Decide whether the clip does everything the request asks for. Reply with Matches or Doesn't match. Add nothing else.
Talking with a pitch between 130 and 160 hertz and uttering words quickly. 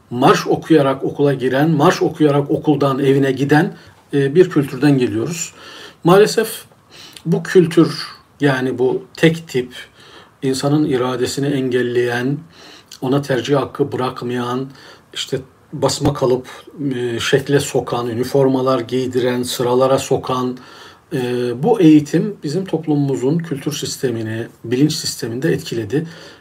Doesn't match